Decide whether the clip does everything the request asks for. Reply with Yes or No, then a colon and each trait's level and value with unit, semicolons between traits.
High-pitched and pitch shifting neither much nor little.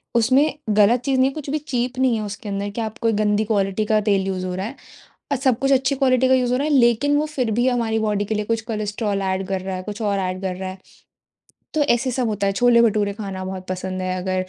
Yes: high, 215 Hz; average, 4.5 semitones